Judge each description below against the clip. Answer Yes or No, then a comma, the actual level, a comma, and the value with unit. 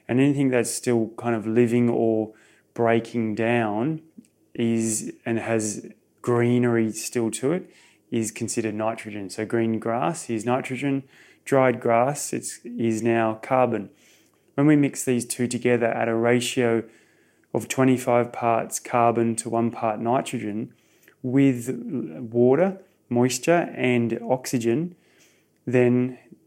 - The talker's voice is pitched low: Yes, low, 120 Hz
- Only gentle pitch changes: Yes, narrow, 1.8 semitones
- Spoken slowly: Yes, slow, 120 wpm